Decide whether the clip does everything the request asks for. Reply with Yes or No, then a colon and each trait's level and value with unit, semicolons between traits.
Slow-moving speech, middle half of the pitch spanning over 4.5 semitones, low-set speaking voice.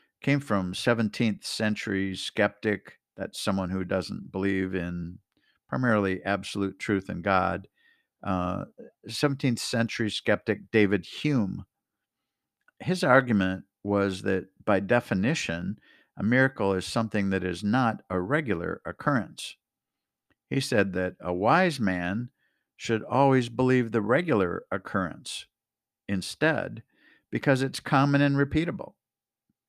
Yes: slow, 115 wpm; average, 5.0 semitones; low, 105 Hz